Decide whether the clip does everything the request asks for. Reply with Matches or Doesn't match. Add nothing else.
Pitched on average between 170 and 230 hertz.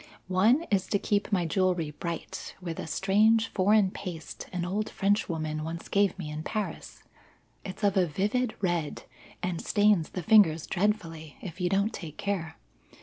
Matches